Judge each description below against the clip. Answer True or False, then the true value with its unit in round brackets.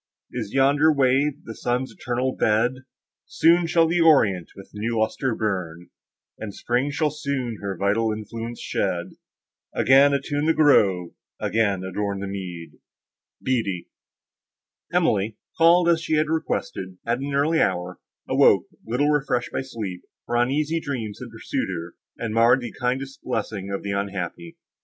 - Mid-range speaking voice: False (120 Hz)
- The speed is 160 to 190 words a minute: False (145 wpm)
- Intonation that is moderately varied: False (6.0 semitones)